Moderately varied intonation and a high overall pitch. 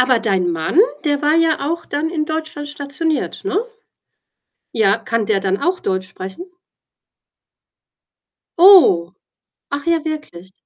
No: wide, 8.6 semitones; very high, 285 Hz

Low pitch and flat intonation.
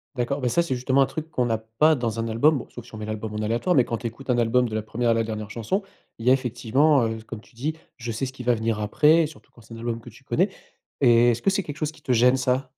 No: low, 120 Hz; average, 3.2 semitones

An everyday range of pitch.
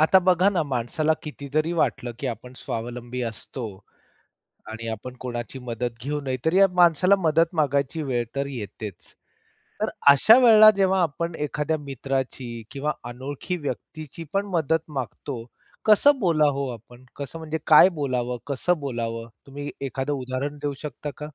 Yes: average, 4.4 semitones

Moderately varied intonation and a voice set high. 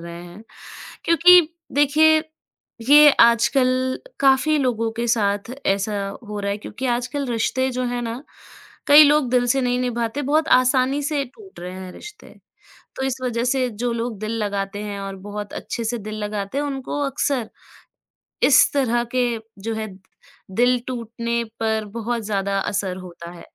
Yes: average, 4.3 semitones; high, 240 Hz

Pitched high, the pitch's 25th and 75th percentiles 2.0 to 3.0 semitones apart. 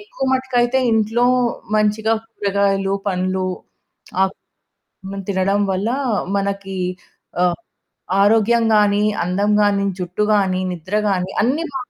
Yes: high, 200 Hz; average, 2.7 semitones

